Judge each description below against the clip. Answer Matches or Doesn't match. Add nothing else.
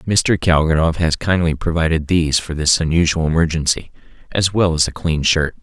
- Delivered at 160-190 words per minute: Matches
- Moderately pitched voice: Doesn't match